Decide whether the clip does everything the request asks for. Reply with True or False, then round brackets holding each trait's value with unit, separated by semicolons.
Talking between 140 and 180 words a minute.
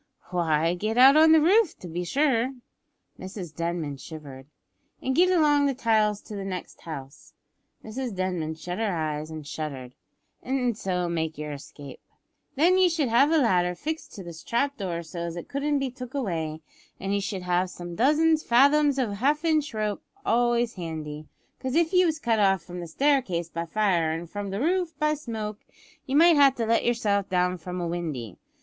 False (190 wpm)